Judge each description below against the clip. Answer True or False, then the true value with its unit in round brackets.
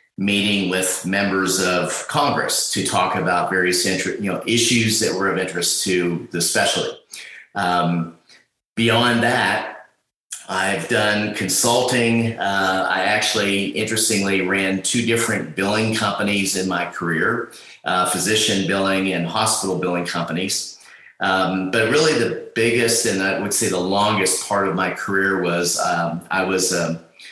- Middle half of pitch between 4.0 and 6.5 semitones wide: False (2.6 semitones)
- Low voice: True (95 Hz)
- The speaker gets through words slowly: False (145 wpm)